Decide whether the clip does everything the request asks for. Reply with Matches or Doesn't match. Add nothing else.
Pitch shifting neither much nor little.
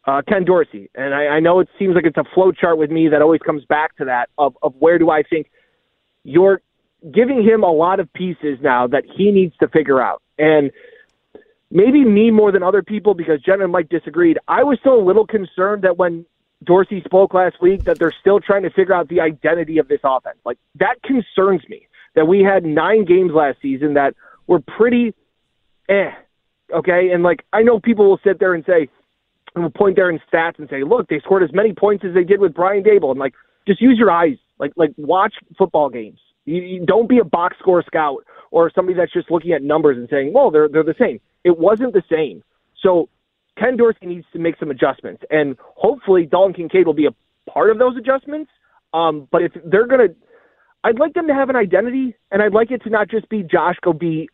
Matches